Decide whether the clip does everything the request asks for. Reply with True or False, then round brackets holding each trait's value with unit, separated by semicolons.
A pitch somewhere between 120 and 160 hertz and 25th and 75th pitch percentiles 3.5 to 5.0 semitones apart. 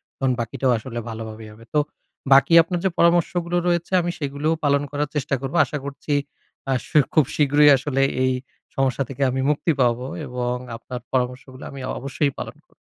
False (140 Hz; 2.9 semitones)